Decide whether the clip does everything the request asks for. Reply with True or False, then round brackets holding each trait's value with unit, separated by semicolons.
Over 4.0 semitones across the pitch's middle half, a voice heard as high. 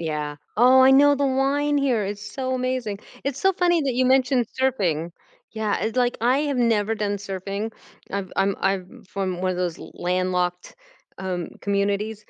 True (5.4 semitones; 215 Hz)